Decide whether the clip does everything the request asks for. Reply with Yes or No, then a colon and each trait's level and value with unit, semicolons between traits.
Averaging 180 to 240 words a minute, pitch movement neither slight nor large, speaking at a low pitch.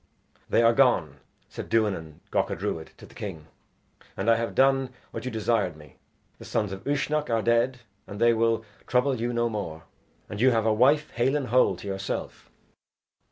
Yes: average, 185 wpm; average, 3.9 semitones; low, 115 Hz